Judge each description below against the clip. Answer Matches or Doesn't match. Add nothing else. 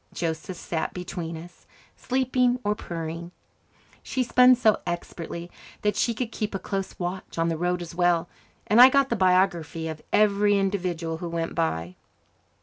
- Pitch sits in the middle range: Matches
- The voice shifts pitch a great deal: Doesn't match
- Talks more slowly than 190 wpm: Matches